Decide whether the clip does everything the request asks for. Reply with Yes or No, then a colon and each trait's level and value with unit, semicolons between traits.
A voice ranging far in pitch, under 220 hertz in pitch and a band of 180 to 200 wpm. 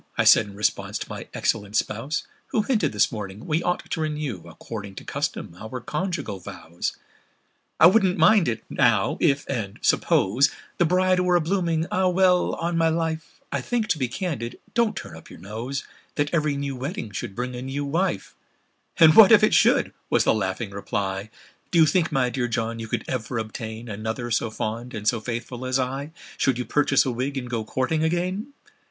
Yes: wide, 6.9 semitones; low, 135 Hz; average, 185 wpm